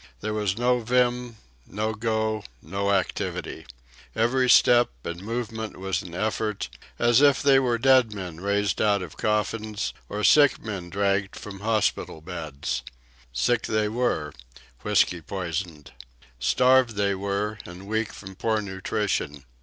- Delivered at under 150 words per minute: Yes, slow, 135 wpm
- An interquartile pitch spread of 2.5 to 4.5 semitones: Yes, average, 3.2 semitones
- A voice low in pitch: Yes, low, 105 Hz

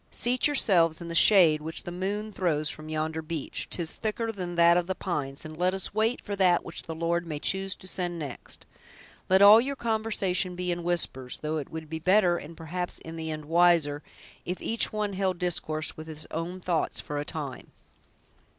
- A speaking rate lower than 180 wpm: No, average, 195 wpm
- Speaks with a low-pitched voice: No, medium, 175 Hz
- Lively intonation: No, average, 3.2 semitones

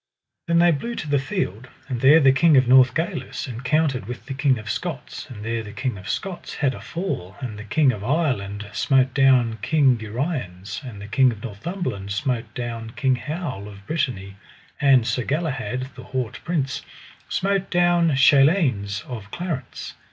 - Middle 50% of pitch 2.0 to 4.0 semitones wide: No, wide, 5.5 semitones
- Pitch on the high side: No, low, 130 Hz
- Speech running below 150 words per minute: No, average, 175 wpm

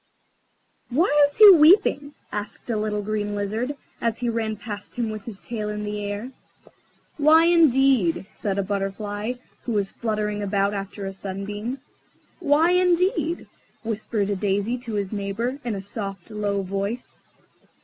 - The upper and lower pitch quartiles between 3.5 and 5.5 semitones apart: Yes, average, 3.9 semitones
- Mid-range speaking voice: No, high, 215 Hz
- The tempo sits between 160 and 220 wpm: No, average, 150 wpm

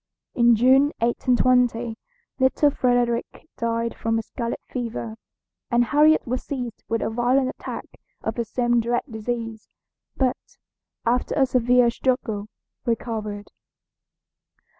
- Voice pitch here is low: No, high, 240 Hz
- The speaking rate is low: Yes, slow, 115 wpm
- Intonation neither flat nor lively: No, narrow, 1.7 semitones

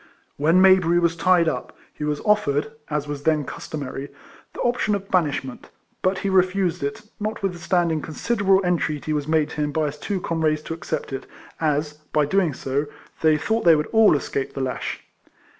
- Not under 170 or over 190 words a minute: Yes, average, 180 wpm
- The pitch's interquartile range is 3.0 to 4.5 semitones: Yes, average, 4.1 semitones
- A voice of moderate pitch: Yes, medium, 160 Hz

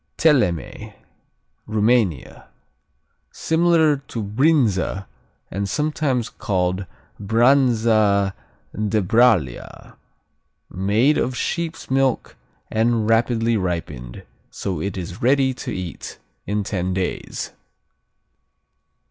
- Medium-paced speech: No, slow, 85 wpm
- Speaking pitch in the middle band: No, low, 110 Hz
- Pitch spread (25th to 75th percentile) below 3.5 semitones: No, average, 5.3 semitones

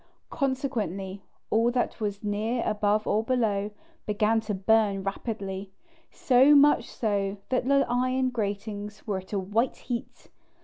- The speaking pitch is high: Yes, high, 215 Hz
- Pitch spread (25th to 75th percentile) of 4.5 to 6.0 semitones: No, average, 3.4 semitones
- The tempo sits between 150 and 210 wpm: No, slow, 135 wpm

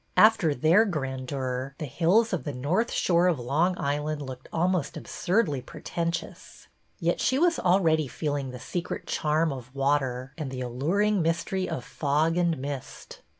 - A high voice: No, medium, 155 Hz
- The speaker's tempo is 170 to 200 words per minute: No, average, 160 wpm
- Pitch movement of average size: Yes, average, 4.7 semitones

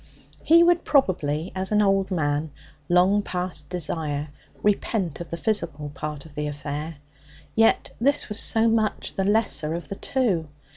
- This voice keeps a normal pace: Yes, average, 155 wpm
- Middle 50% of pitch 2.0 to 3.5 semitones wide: No, wide, 5.6 semitones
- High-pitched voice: No, medium, 180 Hz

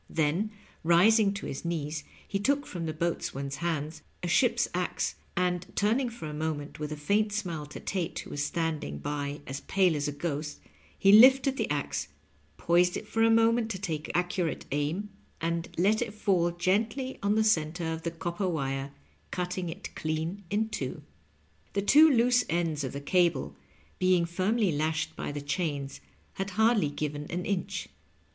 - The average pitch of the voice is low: No, medium, 175 Hz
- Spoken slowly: No, average, 175 wpm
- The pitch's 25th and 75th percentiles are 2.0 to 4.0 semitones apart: No, average, 5.2 semitones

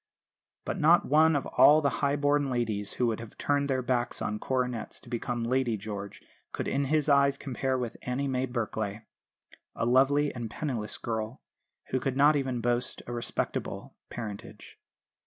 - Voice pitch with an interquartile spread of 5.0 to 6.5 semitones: No, average, 3.2 semitones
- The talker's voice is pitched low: Yes, low, 125 Hz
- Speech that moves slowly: No, average, 170 wpm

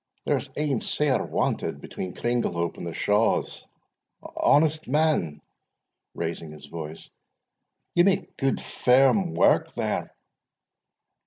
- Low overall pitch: Yes, low, 125 Hz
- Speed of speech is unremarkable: No, slow, 105 wpm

